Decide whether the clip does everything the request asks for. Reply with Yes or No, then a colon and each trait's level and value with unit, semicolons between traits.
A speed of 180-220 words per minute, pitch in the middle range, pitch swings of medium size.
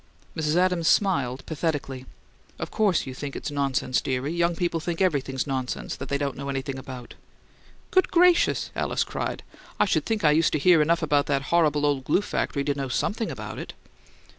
Yes: average, 190 wpm; medium, 145 Hz; average, 3.9 semitones